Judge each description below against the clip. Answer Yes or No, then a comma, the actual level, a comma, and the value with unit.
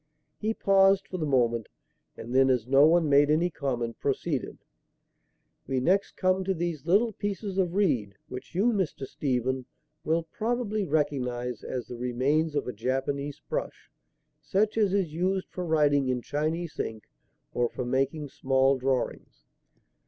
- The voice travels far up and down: Yes, wide, 6.1 semitones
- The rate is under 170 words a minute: Yes, average, 150 wpm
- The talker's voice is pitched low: No, medium, 145 Hz